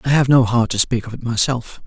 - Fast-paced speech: Yes, fast, 290 wpm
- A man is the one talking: Yes, male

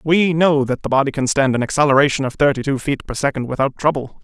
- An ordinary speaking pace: No, fast, 240 wpm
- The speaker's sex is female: No, male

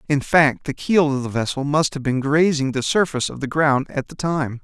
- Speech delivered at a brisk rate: Yes, fast, 245 wpm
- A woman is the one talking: No, male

